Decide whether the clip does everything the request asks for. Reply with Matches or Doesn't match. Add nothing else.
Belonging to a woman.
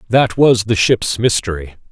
Doesn't match